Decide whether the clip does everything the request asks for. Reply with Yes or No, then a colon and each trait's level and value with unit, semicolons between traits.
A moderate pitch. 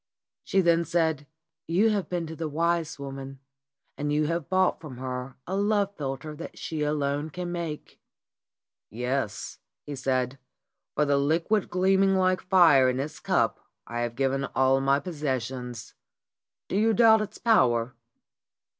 Yes: medium, 150 Hz